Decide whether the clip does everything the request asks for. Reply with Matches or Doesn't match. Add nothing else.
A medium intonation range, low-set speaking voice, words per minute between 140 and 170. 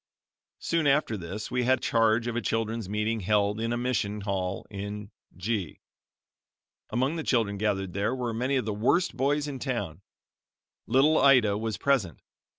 Matches